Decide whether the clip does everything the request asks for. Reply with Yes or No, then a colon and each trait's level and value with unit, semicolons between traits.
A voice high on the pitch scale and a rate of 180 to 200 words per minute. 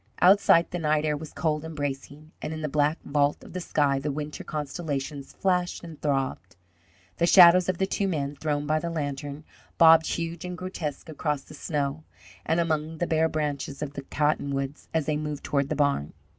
No: medium, 150 Hz; average, 195 wpm